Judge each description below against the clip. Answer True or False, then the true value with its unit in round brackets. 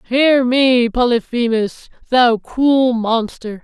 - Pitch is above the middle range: True (245 Hz)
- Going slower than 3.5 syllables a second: True (3.1 syllables/s)